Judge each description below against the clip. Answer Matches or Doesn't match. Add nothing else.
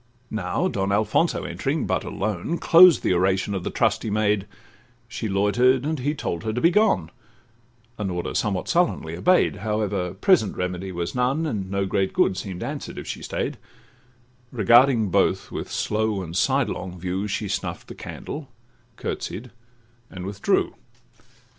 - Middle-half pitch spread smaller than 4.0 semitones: Doesn't match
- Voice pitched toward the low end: Matches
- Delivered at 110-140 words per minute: Doesn't match